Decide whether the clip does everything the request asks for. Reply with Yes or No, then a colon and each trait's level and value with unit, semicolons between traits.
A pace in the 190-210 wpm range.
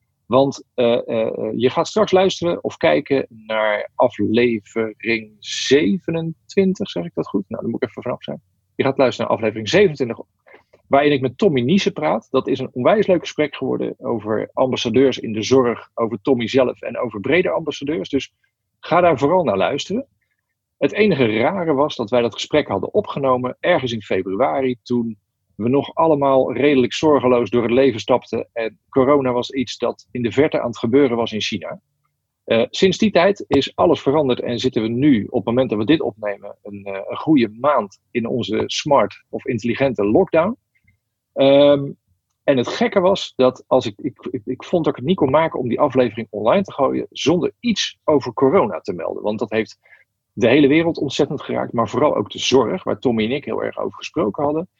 Yes: average, 195 wpm